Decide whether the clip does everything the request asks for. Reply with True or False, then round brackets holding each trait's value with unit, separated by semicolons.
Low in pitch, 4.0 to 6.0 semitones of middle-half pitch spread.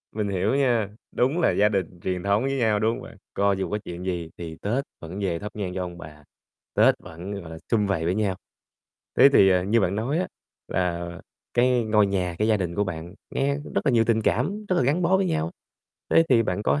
True (100 Hz; 4.8 semitones)